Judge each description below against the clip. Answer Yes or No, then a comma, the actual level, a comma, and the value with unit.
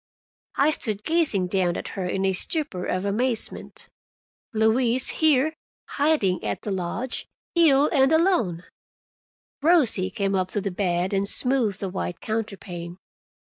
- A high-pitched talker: Yes, high, 210 Hz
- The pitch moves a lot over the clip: Yes, wide, 6.5 semitones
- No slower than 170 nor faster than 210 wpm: No, average, 140 wpm